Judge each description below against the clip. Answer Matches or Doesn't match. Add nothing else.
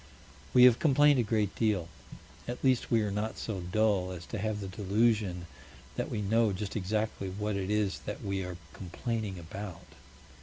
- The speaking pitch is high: Doesn't match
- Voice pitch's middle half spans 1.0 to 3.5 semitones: Matches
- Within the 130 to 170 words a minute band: Doesn't match